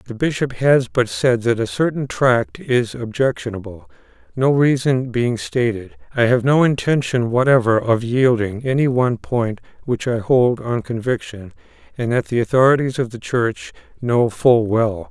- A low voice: Yes, low, 120 Hz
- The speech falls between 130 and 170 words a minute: Yes, average, 160 wpm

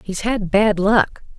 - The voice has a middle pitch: No, high, 205 Hz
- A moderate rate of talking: Yes, average, 175 wpm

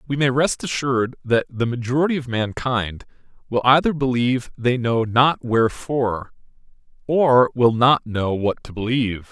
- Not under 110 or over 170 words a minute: Yes, average, 150 wpm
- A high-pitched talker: No, low, 125 Hz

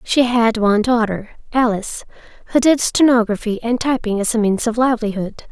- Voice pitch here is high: Yes, high, 230 Hz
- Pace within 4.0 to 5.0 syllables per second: No, 5.5 syllables/s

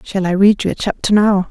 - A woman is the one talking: Yes, female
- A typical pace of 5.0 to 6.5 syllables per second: Yes, 5.7 syllables/s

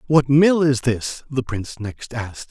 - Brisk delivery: No, average, 190 wpm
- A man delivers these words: Yes, male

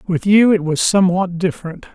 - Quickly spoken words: No, average, 185 wpm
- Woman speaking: No, male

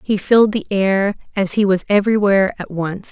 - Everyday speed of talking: Yes, average, 195 wpm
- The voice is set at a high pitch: Yes, high, 200 Hz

